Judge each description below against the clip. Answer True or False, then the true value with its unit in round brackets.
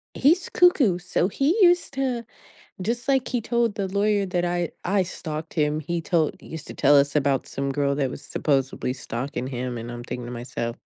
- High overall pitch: False (170 Hz)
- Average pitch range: False (8.3 semitones)